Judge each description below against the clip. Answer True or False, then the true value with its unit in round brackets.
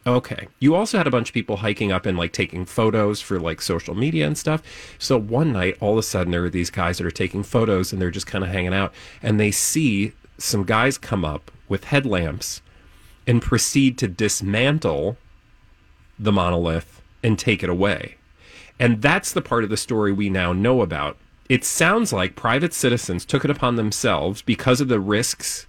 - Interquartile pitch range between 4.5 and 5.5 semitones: True (5.0 semitones)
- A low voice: True (105 Hz)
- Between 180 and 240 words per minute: True (200 wpm)